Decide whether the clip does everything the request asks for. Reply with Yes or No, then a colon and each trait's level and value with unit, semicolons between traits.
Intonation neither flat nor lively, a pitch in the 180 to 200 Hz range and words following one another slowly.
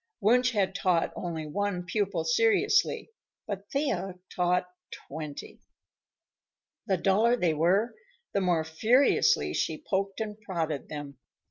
Yes: average, 4.5 semitones; high, 190 Hz; slow, 120 wpm